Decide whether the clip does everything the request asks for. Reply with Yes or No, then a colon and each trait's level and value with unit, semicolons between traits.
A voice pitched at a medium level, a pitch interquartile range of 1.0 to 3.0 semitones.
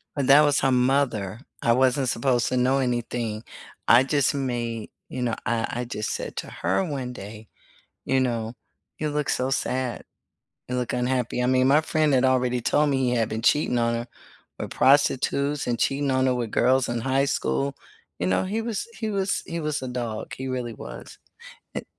No: low, 125 Hz; average, 2.7 semitones